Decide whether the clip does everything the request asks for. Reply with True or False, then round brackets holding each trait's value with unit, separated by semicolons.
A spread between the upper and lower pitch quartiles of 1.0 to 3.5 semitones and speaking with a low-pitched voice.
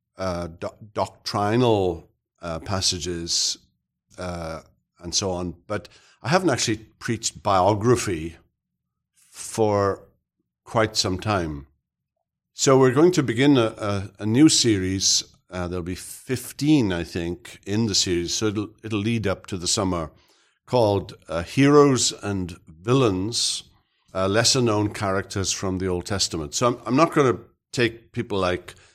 False (4.1 semitones; 100 Hz)